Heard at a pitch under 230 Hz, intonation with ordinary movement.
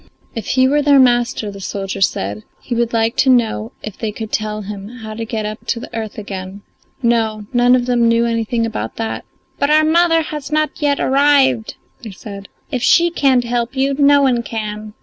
No: high, 235 Hz; average, 3.7 semitones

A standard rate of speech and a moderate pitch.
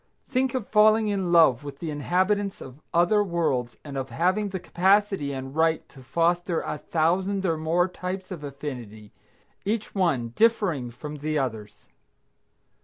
Yes: average, 155 wpm; medium, 170 Hz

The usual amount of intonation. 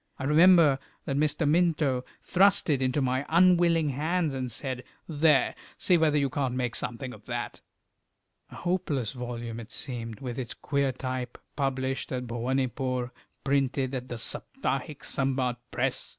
Yes: average, 3.2 semitones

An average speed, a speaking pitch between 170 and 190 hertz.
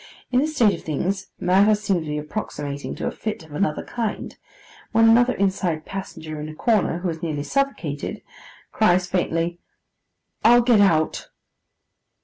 Yes: average, 155 wpm; medium, 185 Hz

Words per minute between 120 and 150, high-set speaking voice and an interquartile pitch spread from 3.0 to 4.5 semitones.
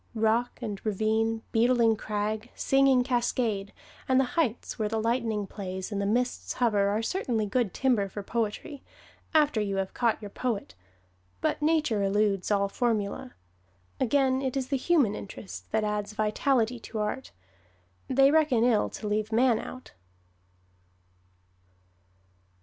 Yes: average, 140 wpm; high, 225 Hz; average, 3.5 semitones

